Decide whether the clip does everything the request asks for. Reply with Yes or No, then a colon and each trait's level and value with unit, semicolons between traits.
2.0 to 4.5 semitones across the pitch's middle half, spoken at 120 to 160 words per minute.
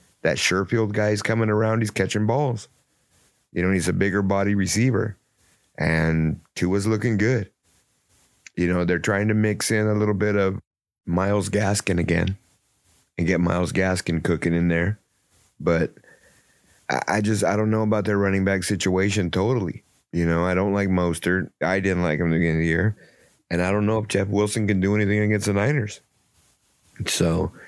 No: average, 2.9 semitones; average, 180 wpm